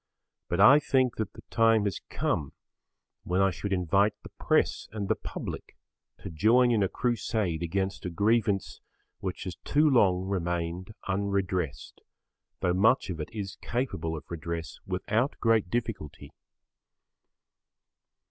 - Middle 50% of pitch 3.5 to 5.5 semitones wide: Yes, average, 4.1 semitones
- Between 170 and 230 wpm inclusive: No, average, 140 wpm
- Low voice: Yes, low, 100 Hz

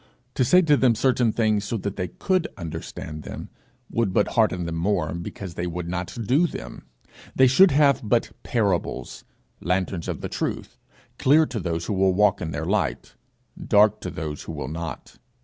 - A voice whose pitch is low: Yes, low, 100 Hz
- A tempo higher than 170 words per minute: Yes, average, 185 wpm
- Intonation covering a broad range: Yes, wide, 6.0 semitones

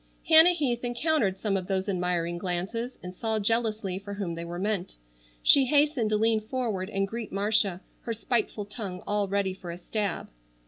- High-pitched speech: Yes, high, 205 Hz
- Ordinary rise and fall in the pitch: Yes, average, 3.6 semitones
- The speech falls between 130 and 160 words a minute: No, average, 180 wpm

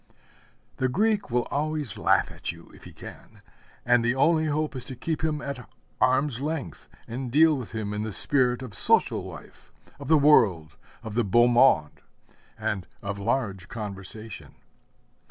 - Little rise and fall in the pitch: No, average, 5.2 semitones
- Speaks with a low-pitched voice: Yes, low, 125 Hz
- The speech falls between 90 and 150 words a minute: No, average, 165 wpm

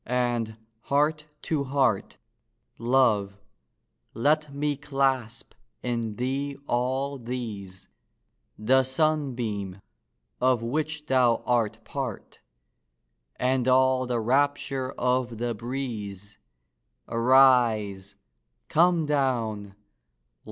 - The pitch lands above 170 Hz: No, low, 125 Hz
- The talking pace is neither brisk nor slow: No, slow, 85 wpm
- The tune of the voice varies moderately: Yes, average, 3.3 semitones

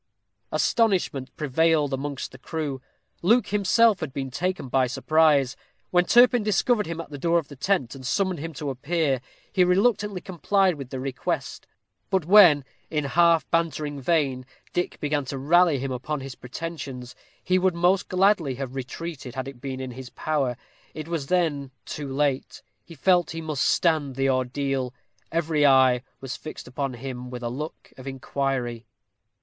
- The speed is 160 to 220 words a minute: Yes, average, 170 wpm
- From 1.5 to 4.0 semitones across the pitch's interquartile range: No, average, 4.5 semitones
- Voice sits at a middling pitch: Yes, medium, 145 Hz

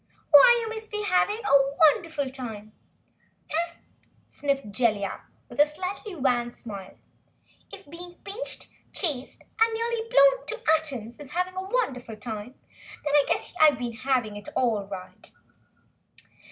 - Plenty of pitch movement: Yes, wide, 8.6 semitones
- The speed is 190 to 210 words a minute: No, average, 140 wpm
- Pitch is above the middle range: Yes, very high, 290 Hz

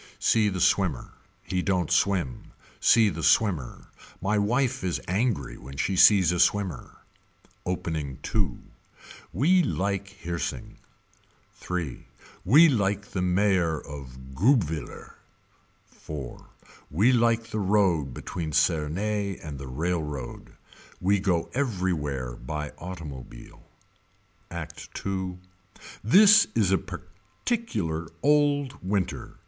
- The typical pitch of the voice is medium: No, very low, 90 Hz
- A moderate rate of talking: No, slow, 110 wpm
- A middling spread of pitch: Yes, average, 5.0 semitones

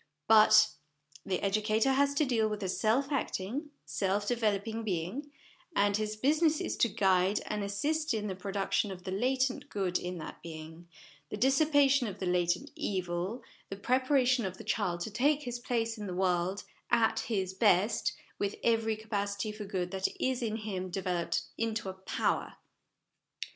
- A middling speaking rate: Yes, average, 165 wpm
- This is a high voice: Yes, high, 210 Hz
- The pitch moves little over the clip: No, average, 4.3 semitones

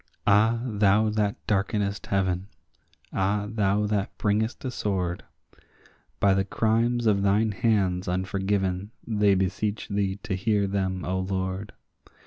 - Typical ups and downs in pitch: No, narrow, 1.9 semitones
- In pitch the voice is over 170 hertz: No, low, 100 Hz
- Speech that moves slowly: Yes, slow, 120 wpm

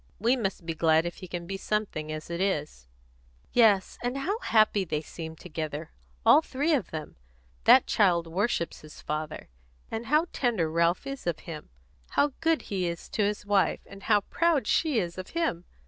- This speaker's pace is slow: No, average, 185 wpm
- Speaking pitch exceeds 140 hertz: Yes, high, 190 Hz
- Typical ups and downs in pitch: No, wide, 6.4 semitones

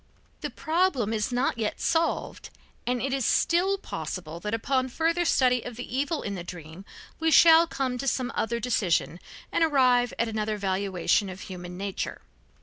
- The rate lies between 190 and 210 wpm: No, average, 170 wpm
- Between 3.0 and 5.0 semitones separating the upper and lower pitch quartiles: No, wide, 5.6 semitones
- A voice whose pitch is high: Yes, high, 245 Hz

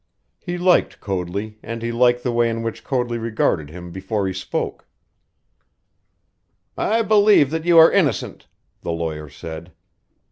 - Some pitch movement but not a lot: No, wide, 7.6 semitones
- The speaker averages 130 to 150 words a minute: Yes, average, 145 wpm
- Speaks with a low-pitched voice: Yes, low, 115 Hz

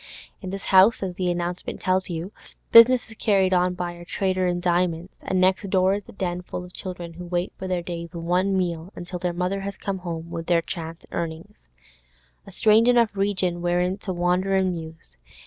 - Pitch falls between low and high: Yes, medium, 180 Hz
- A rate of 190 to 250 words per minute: Yes, average, 200 wpm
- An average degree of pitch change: No, narrow, 1.6 semitones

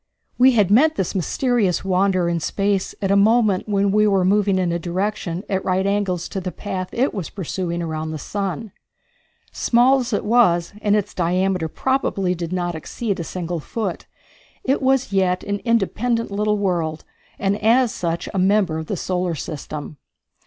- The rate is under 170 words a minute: No, average, 175 wpm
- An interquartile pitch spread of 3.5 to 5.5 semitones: No, average, 3.1 semitones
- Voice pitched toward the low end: No, high, 195 Hz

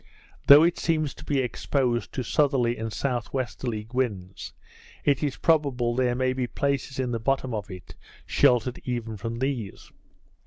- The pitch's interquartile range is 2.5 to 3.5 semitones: Yes, average, 2.9 semitones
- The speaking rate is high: No, average, 155 wpm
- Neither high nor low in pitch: No, low, 125 Hz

